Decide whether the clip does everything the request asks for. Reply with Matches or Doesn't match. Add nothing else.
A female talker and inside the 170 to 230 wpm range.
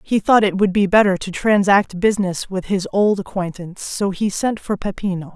Matches